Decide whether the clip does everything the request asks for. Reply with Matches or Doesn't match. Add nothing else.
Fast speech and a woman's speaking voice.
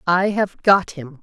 Doesn't match